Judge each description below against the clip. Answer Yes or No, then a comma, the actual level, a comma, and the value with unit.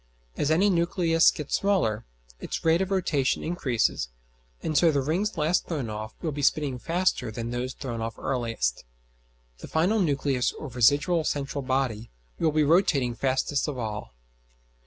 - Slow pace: No, average, 155 wpm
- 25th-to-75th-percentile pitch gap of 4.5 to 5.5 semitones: Yes, average, 5.1 semitones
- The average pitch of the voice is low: No, medium, 145 Hz